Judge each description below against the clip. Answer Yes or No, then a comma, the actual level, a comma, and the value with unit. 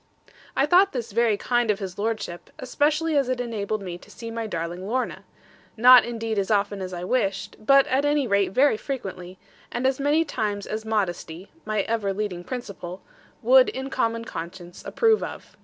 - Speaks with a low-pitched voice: No, high, 220 Hz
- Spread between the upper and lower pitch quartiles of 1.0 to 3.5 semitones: No, average, 4.7 semitones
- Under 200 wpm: Yes, average, 180 wpm